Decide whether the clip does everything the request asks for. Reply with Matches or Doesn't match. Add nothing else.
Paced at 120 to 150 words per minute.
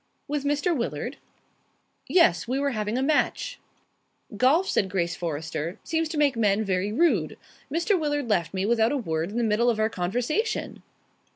Doesn't match